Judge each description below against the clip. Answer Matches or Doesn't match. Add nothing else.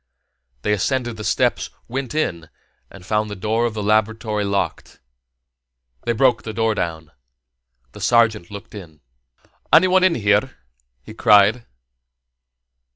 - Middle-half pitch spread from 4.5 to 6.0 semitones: Doesn't match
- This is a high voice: Doesn't match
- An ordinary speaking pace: Doesn't match